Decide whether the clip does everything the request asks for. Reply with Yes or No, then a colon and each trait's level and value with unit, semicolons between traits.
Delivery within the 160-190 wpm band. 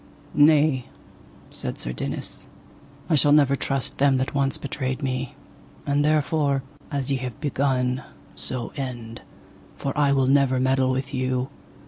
No: average, 140 wpm